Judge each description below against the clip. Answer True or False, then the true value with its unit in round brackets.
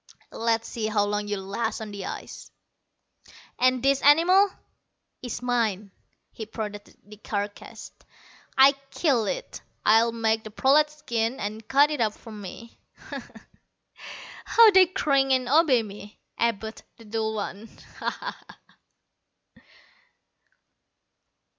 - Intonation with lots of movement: False (4.3 semitones)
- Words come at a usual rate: False (125 wpm)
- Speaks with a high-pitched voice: True (230 Hz)